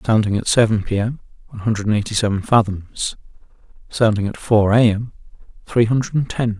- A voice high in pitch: No, low, 110 Hz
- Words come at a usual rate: Yes, average, 165 wpm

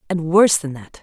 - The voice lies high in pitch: No, medium, 165 Hz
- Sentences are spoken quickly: Yes, fast, 235 wpm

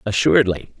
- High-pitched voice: No, low, 100 Hz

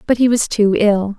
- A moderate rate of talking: No, fast, 255 wpm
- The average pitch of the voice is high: Yes, high, 215 Hz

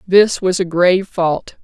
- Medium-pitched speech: Yes, medium, 180 Hz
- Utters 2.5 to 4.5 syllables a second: Yes, 4.1 syllables/s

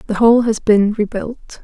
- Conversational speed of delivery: Yes, average, 185 wpm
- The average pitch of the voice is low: No, high, 220 Hz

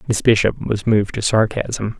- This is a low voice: Yes, low, 105 Hz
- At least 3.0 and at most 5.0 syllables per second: Yes, 4.9 syllables/s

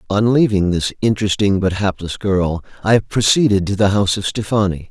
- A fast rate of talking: No, average, 170 wpm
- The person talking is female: No, male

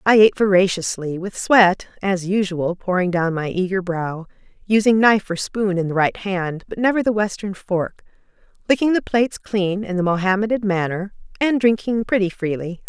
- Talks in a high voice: Yes, high, 195 Hz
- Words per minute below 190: Yes, average, 170 wpm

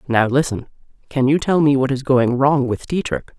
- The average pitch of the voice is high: No, low, 135 Hz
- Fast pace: Yes, fast, 210 wpm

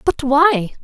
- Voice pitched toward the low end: No, very high, 285 Hz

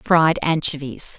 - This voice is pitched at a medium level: Yes, medium, 155 Hz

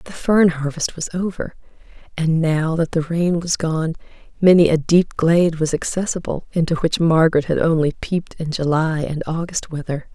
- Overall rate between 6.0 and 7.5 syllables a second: No, 5.0 syllables/s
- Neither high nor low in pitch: Yes, medium, 165 Hz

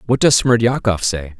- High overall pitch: No, low, 110 Hz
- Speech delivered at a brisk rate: No, average, 170 wpm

